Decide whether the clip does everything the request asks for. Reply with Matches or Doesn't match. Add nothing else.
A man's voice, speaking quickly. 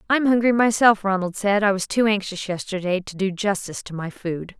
Doesn't match